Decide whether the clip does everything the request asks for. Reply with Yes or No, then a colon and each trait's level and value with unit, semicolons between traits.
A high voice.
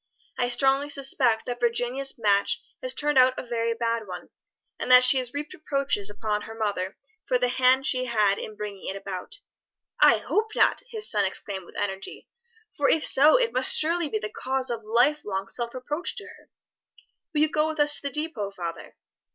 Yes: very high, 250 Hz